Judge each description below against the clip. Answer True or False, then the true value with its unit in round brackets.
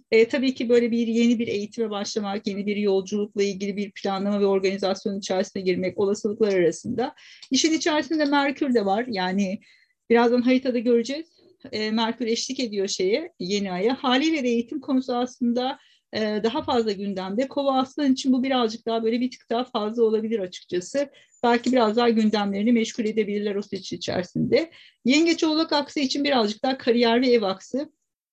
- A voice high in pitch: True (235 Hz)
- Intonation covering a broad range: False (4.1 semitones)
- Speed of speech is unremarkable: False (165 wpm)